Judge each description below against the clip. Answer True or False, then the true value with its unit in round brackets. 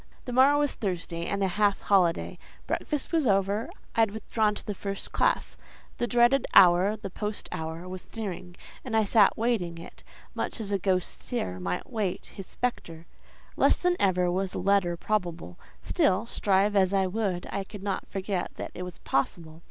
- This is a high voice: True (195 Hz)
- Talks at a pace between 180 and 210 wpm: True (185 wpm)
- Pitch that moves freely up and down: False (3.4 semitones)